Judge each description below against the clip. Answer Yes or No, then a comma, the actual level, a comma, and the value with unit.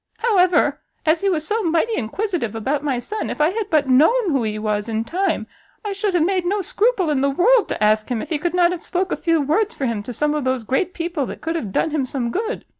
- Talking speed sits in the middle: No, fast, 265 wpm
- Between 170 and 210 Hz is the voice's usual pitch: No, very high, 320 Hz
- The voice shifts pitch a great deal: Yes, wide, 6.7 semitones